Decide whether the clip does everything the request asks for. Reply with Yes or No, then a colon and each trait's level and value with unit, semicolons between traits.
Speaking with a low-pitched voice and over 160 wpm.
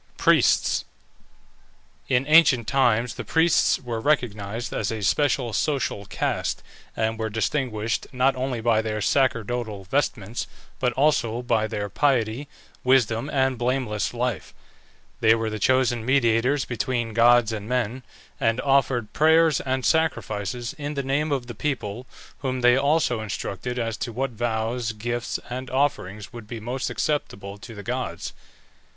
No: low, 120 Hz; average, 145 wpm